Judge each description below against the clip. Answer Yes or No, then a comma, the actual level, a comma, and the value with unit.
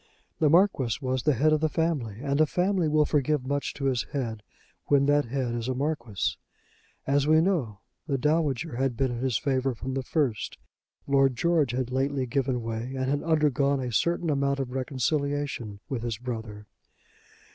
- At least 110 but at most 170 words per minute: No, average, 180 wpm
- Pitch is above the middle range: No, low, 135 Hz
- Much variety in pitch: No, average, 3.2 semitones